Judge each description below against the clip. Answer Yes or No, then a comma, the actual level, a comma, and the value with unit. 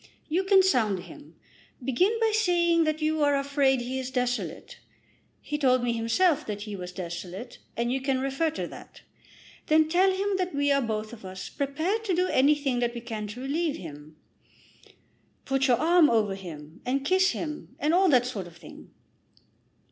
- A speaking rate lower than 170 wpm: No, average, 185 wpm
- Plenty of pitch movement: Yes, wide, 6.0 semitones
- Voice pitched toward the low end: No, very high, 270 Hz